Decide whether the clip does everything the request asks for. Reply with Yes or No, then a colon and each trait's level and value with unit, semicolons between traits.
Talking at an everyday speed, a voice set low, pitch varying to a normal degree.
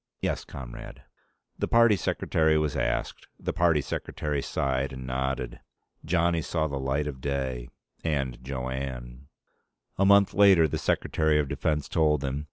Yes: average, 150 wpm; very low, 70 Hz; average, 3.2 semitones